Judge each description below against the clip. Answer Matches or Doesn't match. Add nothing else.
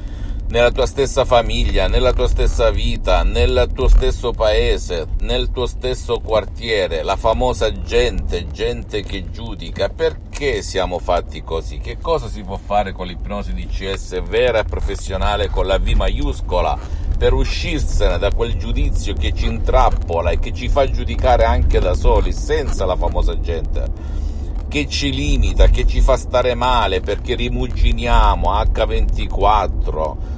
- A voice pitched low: Matches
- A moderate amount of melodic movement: Doesn't match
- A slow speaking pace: Doesn't match